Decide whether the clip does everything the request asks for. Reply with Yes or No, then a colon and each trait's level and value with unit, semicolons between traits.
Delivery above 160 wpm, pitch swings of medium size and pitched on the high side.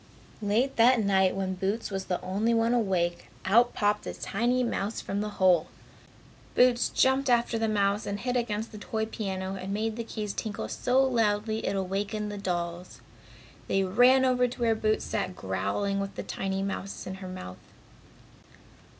Yes: average, 175 wpm; average, 3.2 semitones; high, 205 Hz